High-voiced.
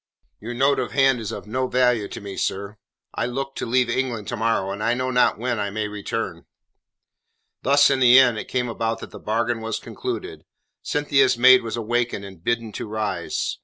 No: low, 120 Hz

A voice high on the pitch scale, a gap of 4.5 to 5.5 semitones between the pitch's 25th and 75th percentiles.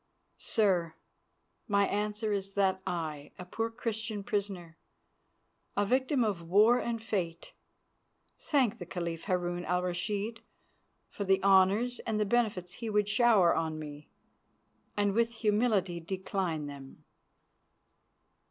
No: high, 200 Hz; average, 3.7 semitones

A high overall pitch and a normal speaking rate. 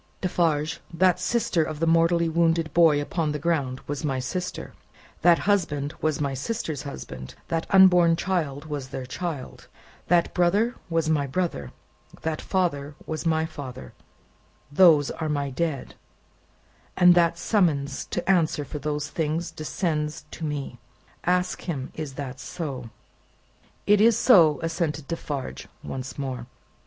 No: medium, 160 Hz; average, 145 wpm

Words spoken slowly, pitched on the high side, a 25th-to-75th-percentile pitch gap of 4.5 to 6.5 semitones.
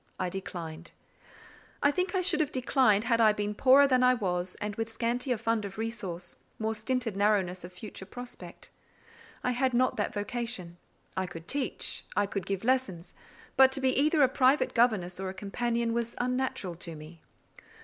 No: average, 180 wpm; high, 225 Hz; average, 5.0 semitones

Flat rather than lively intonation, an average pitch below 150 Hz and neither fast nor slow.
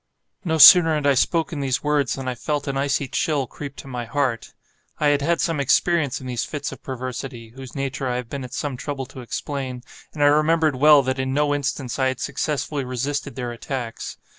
No: narrow, 2.3 semitones; medium, 140 Hz; fast, 215 wpm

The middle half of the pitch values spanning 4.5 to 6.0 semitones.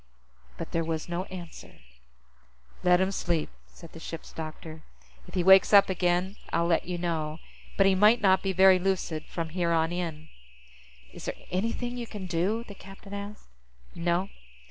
No: narrow, 2.6 semitones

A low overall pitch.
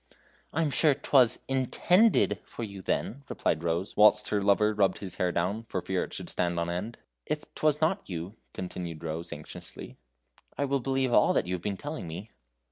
Yes: low, 105 Hz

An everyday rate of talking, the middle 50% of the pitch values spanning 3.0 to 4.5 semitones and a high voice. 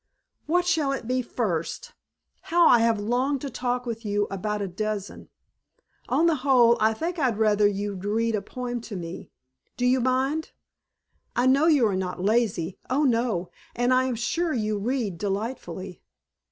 Yes: average, 170 wpm; average, 4.0 semitones; high, 235 Hz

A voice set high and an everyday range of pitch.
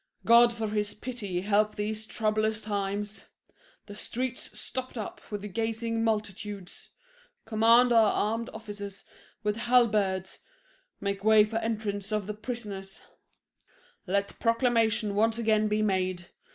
No: high, 215 Hz; narrow, 1.9 semitones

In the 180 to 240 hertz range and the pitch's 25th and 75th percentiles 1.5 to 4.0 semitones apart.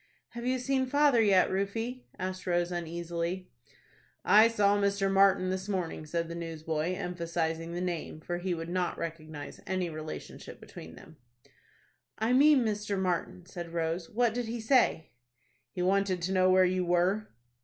Yes: medium, 185 Hz; average, 3.4 semitones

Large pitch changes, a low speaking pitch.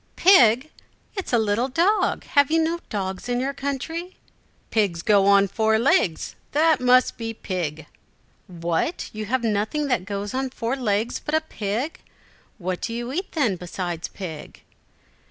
No: wide, 5.9 semitones; high, 230 Hz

